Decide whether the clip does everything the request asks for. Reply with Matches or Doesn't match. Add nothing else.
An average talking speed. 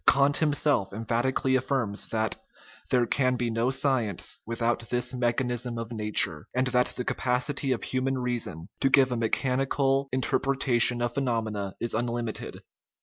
Matches